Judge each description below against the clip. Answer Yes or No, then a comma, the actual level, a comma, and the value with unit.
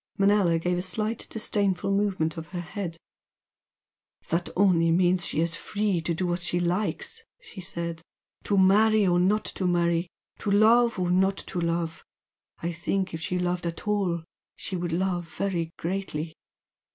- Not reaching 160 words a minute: No, average, 165 wpm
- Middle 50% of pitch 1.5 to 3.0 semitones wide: Yes, narrow, 2.6 semitones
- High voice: No, medium, 180 Hz